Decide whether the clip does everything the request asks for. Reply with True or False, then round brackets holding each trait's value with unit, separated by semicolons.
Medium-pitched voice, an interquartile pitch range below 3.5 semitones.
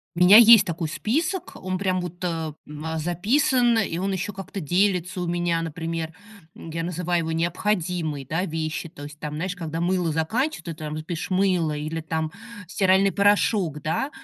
True (175 Hz; 3.0 semitones)